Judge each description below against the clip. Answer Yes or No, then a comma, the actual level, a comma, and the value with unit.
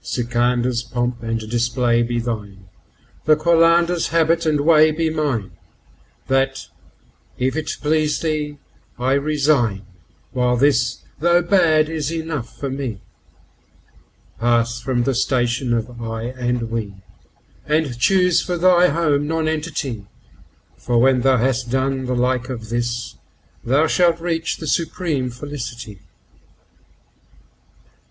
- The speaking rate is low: Yes, slow, 115 wpm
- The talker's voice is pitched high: No, low, 130 Hz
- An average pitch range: Yes, average, 4.7 semitones